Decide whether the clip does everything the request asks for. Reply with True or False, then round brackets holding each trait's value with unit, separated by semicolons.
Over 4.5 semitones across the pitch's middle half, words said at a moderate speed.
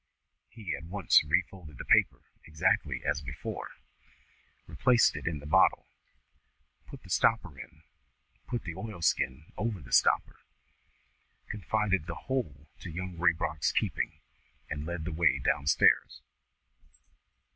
False (5.1 semitones; 125 wpm)